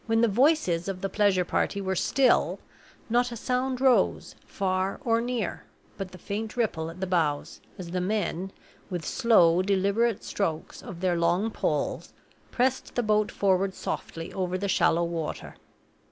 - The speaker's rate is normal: Yes, average, 160 wpm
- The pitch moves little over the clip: No, average, 4.1 semitones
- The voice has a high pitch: Yes, high, 195 Hz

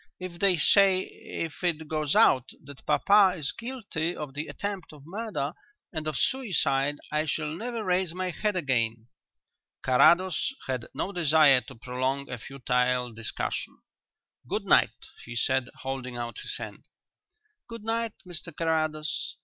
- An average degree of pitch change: No, wide, 5.7 semitones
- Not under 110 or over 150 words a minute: Yes, average, 145 wpm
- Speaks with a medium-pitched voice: Yes, medium, 155 Hz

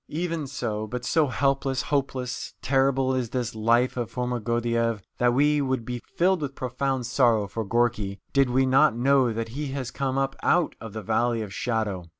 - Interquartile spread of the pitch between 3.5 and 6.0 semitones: No, average, 2.8 semitones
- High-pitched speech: No, low, 125 Hz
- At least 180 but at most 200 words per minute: Yes, average, 185 wpm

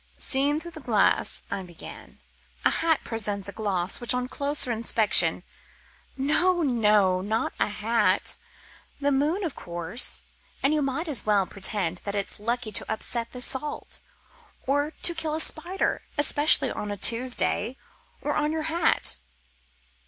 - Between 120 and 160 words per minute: Yes, average, 150 wpm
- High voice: Yes, high, 245 Hz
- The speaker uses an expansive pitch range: Yes, wide, 6.3 semitones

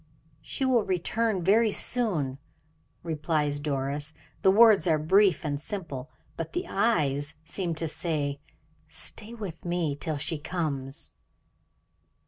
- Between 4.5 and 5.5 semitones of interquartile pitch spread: Yes, average, 5.2 semitones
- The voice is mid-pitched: Yes, medium, 165 Hz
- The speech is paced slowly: Yes, slow, 120 wpm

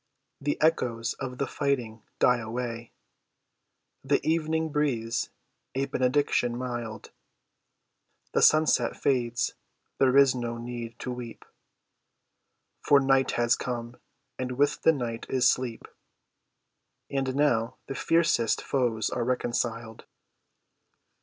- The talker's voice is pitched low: Yes, low, 125 Hz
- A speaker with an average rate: No, slow, 110 wpm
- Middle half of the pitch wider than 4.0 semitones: No, average, 2.7 semitones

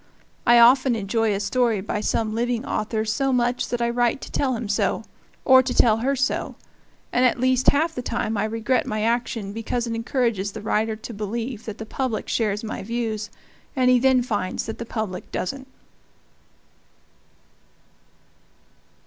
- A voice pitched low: No, high, 230 Hz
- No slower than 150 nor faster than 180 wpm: Yes, average, 170 wpm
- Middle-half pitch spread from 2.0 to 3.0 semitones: Yes, narrow, 2.5 semitones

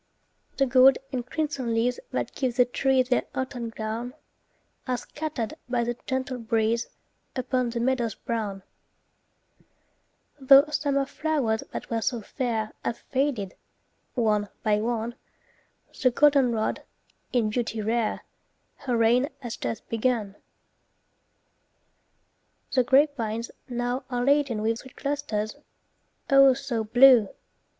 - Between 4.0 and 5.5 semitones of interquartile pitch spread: No, average, 2.7 semitones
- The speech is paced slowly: Yes, slow, 120 wpm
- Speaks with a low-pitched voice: No, high, 245 Hz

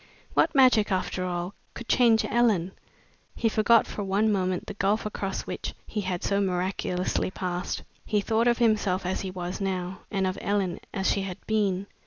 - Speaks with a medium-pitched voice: No, high, 195 Hz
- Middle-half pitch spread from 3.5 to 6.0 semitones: No, average, 2.8 semitones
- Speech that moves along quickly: No, average, 180 wpm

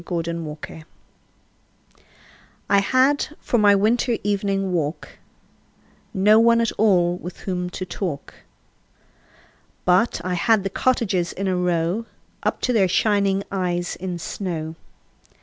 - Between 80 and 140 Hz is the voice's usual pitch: No, high, 190 Hz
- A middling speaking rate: No, slow, 125 wpm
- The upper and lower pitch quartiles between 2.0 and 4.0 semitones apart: Yes, average, 3.2 semitones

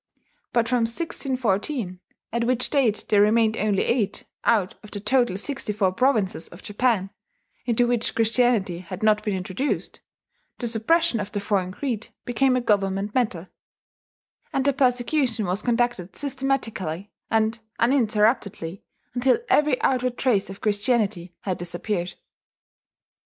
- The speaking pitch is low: No, high, 220 Hz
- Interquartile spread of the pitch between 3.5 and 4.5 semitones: Yes, average, 4.1 semitones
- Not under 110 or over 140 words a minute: Yes, slow, 135 wpm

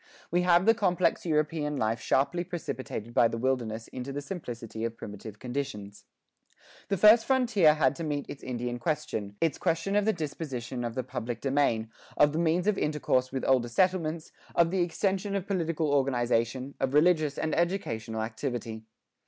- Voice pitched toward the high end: No, medium, 145 Hz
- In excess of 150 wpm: Yes, average, 170 wpm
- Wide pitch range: Yes, wide, 6.2 semitones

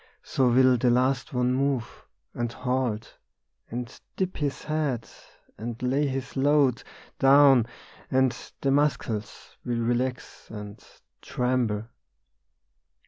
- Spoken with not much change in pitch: Yes, narrow, 2.2 semitones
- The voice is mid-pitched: No, low, 125 Hz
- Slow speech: Yes, slow, 110 wpm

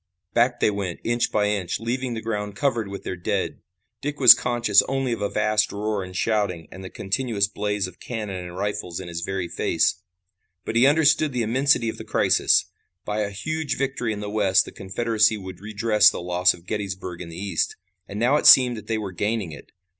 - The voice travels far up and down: No, average, 3.7 semitones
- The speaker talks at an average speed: No, fast, 210 wpm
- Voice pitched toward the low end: Yes, low, 105 Hz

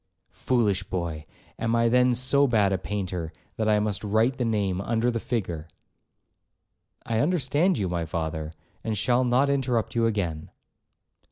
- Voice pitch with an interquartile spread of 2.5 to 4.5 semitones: No, average, 4.9 semitones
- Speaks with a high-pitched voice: No, low, 110 Hz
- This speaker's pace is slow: No, average, 150 wpm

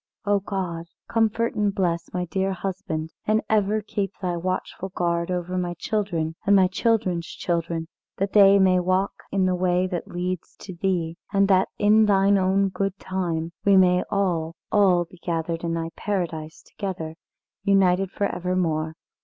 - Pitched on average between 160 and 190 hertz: Yes, medium, 185 Hz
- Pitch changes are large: No, narrow, 2.5 semitones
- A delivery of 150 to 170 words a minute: Yes, average, 160 wpm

